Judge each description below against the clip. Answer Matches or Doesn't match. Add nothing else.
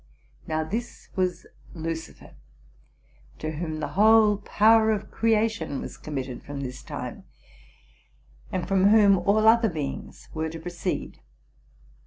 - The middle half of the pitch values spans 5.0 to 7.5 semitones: Matches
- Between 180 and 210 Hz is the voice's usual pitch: Matches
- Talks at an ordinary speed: Doesn't match